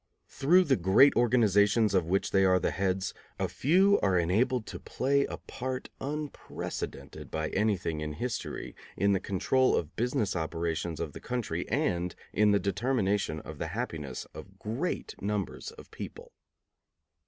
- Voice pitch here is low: Yes, low, 100 Hz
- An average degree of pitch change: No, wide, 6.2 semitones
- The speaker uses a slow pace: No, average, 155 wpm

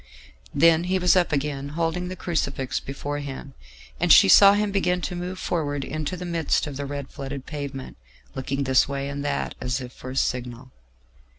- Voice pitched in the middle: Yes, medium, 145 Hz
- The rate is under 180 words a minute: No, average, 190 wpm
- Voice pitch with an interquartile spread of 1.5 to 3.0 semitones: No, average, 4.2 semitones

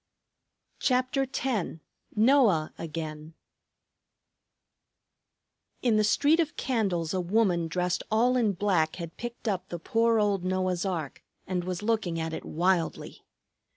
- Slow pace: Yes, slow, 125 wpm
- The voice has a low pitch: No, high, 190 Hz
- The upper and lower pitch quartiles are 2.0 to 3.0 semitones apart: No, average, 5.0 semitones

